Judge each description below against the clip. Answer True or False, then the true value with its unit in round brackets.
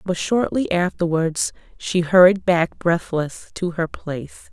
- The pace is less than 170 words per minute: True (135 wpm)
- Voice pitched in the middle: True (175 Hz)